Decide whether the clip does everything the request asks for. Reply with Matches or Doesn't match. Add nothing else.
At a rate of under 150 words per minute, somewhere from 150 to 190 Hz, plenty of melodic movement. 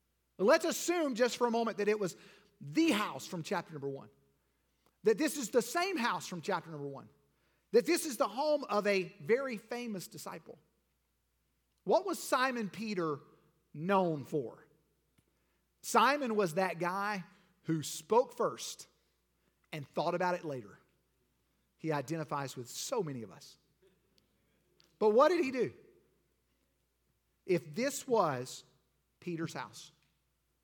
Matches